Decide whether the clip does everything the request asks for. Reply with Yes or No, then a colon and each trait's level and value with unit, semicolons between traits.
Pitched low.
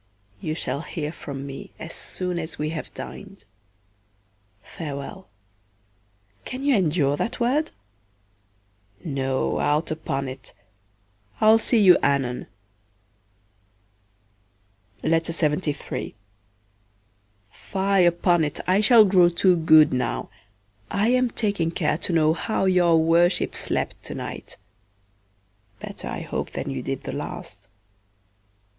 No: medium, 160 Hz